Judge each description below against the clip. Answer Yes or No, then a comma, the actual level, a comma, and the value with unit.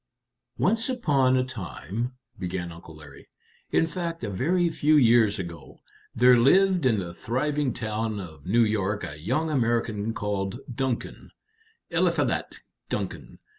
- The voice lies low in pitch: Yes, low, 115 Hz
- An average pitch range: No, wide, 6.5 semitones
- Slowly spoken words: Yes, slow, 130 wpm